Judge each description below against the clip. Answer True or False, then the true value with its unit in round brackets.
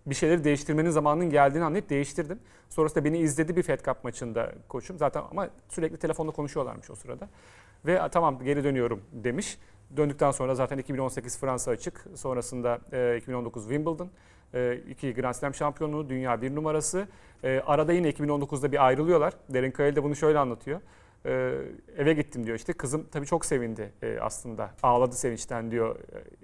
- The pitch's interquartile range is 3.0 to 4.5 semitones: True (4.0 semitones)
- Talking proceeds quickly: True (160 wpm)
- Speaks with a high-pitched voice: False (140 Hz)